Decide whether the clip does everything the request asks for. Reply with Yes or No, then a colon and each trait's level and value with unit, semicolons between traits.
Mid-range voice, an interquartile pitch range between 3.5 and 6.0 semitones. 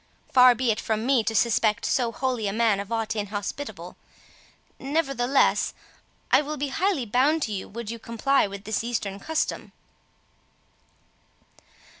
No: high, 235 Hz; average, 4.1 semitones